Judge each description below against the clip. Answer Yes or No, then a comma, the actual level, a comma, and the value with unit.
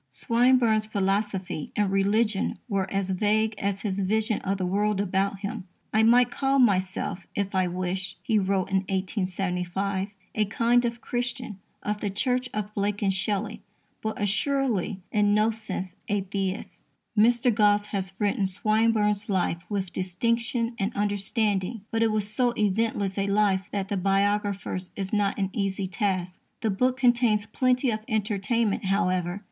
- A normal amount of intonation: No, narrow, 2.3 semitones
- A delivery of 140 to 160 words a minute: Yes, average, 155 wpm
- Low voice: No, high, 205 Hz